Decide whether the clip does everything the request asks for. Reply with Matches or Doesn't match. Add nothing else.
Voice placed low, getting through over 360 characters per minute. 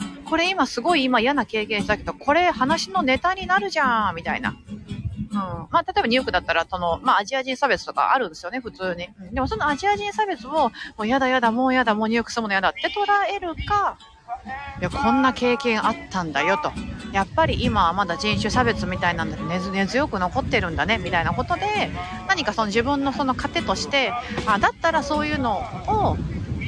Doesn't match